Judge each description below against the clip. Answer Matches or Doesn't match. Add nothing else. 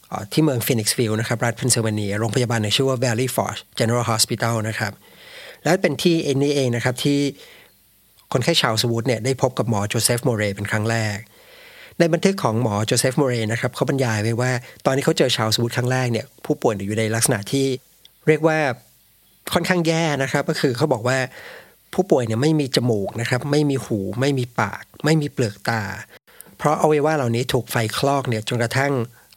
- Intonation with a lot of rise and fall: Doesn't match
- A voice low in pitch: Matches